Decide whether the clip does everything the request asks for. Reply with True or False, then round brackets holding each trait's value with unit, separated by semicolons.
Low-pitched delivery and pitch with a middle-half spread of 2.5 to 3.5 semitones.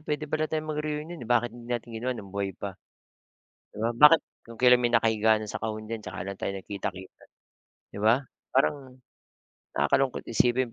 False (120 Hz; 4.0 semitones)